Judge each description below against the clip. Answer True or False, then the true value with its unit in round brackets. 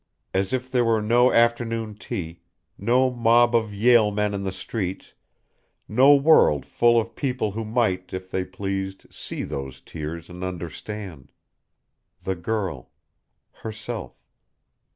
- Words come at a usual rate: False (130 wpm)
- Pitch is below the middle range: True (105 Hz)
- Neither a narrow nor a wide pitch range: True (4.2 semitones)